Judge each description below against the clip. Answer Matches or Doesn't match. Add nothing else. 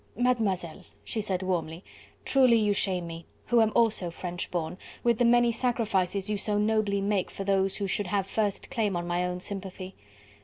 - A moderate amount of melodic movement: Matches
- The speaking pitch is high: Matches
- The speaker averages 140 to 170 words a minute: Doesn't match